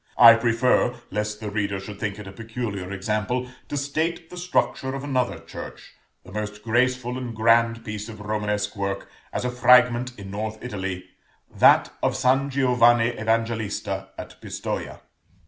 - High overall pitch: No, low, 115 Hz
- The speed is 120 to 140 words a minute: No, average, 155 wpm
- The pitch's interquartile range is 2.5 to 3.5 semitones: Yes, average, 3.2 semitones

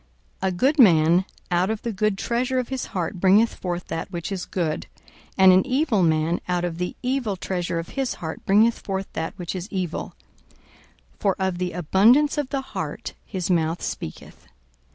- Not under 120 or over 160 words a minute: No, average, 185 wpm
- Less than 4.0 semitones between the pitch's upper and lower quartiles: No, average, 4.6 semitones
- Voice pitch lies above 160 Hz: Yes, high, 190 Hz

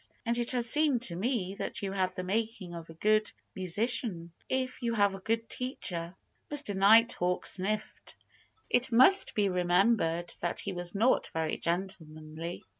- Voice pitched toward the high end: Yes, high, 195 Hz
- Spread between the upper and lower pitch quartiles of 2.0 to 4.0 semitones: No, average, 4.8 semitones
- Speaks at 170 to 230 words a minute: No, average, 160 wpm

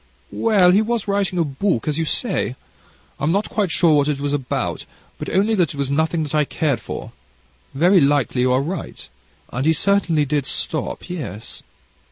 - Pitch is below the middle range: No, medium, 160 Hz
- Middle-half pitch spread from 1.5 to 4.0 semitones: No, average, 5.0 semitones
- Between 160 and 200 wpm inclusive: Yes, average, 190 wpm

